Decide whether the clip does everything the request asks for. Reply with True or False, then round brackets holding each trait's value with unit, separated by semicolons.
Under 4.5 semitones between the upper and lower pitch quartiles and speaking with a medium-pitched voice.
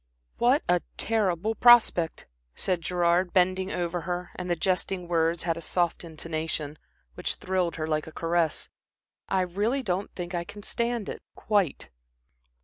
True (2.5 semitones; 180 Hz)